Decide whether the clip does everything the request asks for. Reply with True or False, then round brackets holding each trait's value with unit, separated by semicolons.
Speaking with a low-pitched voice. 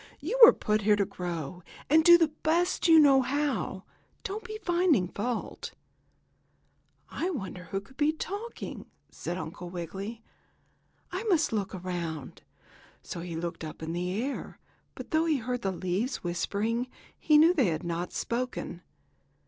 False (225 Hz)